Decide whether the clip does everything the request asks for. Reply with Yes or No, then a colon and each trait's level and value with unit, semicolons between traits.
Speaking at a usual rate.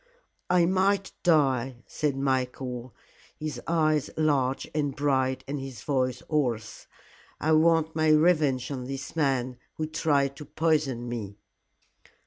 No: slow, 125 wpm